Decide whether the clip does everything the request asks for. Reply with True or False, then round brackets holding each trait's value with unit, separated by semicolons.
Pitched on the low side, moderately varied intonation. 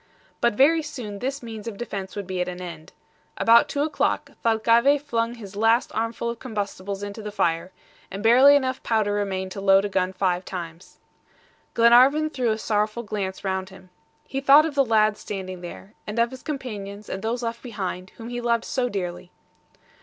False (215 Hz; 3.8 semitones)